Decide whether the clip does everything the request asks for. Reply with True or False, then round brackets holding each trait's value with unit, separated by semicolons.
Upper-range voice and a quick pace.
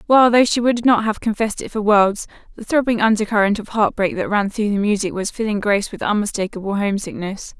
True (210 Hz; 215 wpm)